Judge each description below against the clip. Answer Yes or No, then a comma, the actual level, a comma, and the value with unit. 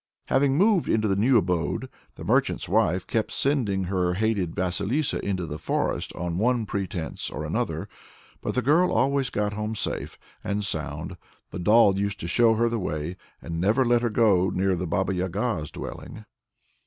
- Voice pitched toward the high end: No, low, 100 Hz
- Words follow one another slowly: No, average, 175 wpm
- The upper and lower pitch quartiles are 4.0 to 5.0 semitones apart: Yes, average, 4.5 semitones